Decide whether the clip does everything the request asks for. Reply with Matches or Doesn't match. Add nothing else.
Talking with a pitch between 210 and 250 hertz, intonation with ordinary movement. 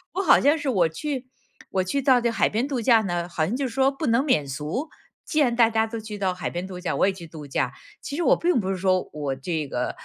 Doesn't match